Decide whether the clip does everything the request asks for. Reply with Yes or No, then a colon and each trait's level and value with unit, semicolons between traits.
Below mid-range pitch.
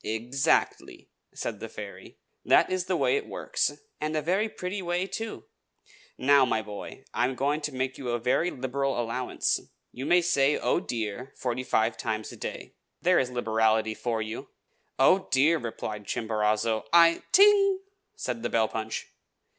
Yes: low, 130 Hz